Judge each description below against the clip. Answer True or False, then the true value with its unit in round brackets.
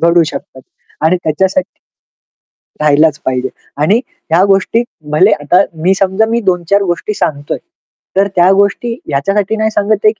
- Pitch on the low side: False (185 Hz)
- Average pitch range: True (4.5 semitones)